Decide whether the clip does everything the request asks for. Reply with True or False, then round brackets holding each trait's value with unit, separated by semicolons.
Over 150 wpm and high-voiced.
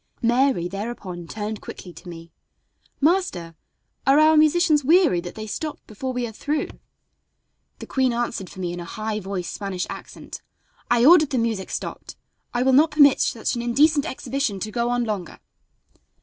True (170 wpm; 235 Hz)